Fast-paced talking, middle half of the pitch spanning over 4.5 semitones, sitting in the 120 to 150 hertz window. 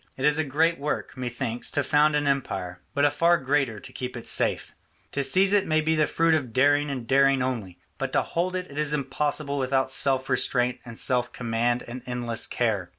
No: fast, 210 wpm; average, 3.3 semitones; low, 135 Hz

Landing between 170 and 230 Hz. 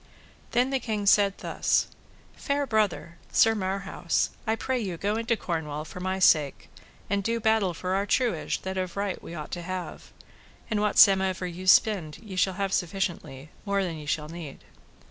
Yes: high, 190 Hz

